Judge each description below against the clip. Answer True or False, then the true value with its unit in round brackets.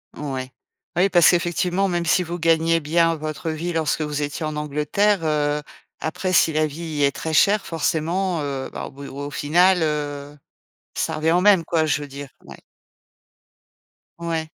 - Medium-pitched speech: True (160 Hz)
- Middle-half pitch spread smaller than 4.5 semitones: True (2.7 semitones)